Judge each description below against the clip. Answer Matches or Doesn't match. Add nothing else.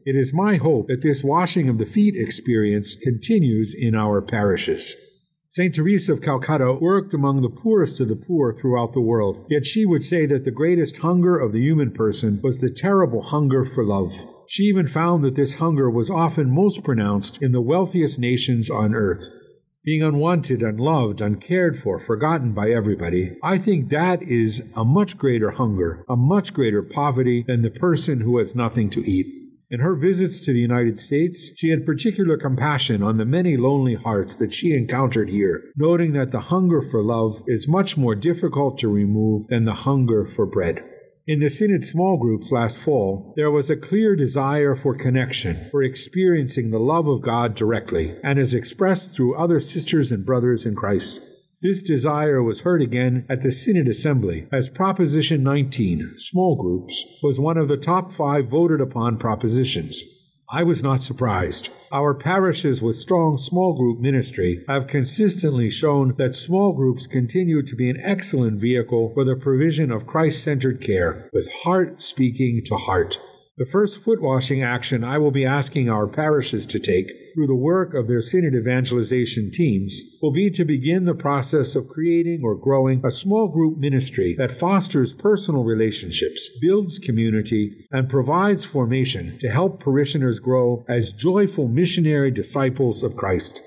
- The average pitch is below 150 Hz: Matches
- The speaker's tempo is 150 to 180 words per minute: Matches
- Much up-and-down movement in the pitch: Matches